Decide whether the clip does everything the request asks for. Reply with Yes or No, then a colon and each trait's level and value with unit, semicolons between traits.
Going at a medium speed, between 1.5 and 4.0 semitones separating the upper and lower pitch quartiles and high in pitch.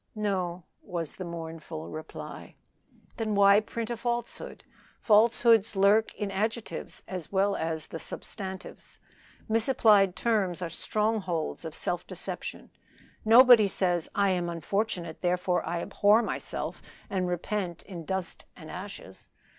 No: slow, 125 wpm; average, 3.7 semitones; high, 195 Hz